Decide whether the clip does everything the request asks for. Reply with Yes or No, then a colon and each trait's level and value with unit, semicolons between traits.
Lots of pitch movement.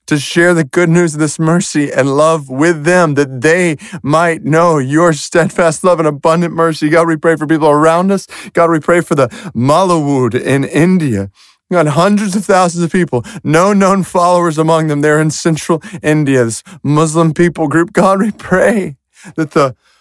No: narrow, 2.4 semitones